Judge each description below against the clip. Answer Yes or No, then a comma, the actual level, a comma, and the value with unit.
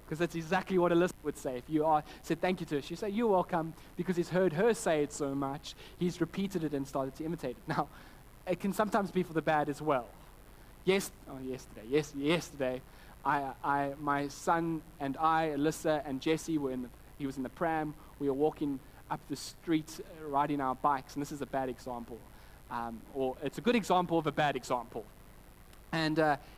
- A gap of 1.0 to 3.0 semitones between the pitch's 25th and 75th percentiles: No, average, 3.5 semitones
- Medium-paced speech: No, fast, 210 wpm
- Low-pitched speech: No, medium, 150 Hz